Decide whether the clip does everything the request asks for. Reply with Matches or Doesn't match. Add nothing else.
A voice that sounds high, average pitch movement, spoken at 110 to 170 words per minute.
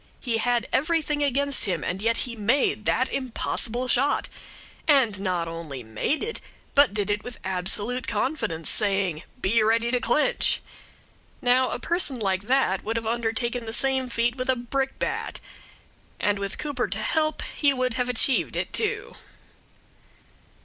Matches